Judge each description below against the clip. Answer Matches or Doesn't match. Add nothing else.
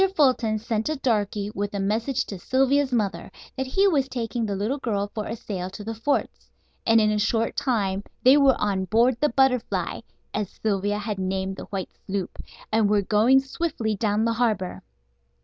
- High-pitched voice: Matches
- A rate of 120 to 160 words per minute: Doesn't match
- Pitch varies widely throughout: Doesn't match